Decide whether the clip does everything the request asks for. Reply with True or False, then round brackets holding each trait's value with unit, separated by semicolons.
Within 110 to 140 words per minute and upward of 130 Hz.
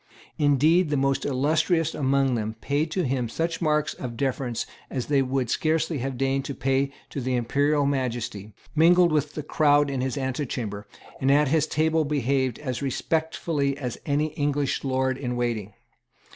False (165 wpm; 140 Hz)